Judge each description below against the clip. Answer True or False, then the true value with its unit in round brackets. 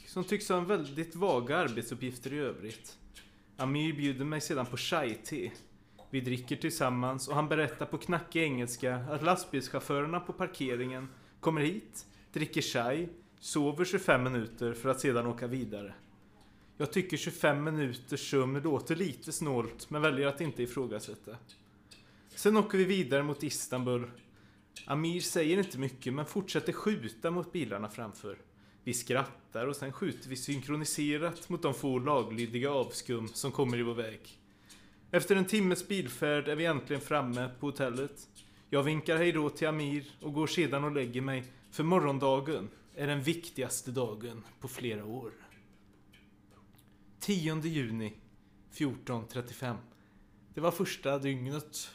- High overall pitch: False (135 Hz)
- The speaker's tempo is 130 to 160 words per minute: True (140 wpm)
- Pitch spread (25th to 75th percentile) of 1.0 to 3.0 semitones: False (4.9 semitones)